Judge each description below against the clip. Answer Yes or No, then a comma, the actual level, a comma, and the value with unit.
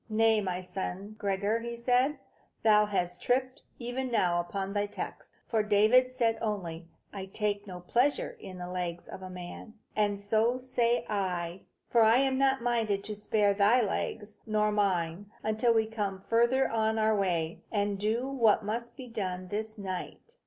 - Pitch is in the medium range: No, high, 210 Hz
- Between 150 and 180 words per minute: Yes, average, 170 wpm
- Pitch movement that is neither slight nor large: Yes, average, 3.3 semitones